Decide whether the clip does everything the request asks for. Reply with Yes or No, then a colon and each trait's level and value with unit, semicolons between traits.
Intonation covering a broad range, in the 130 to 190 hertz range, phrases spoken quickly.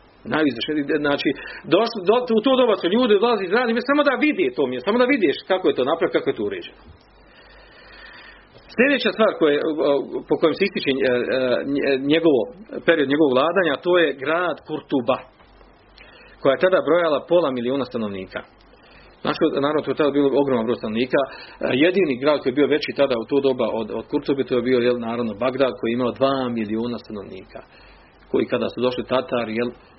Yes: wide, 8.2 semitones; medium, 140 Hz; fast, 180 wpm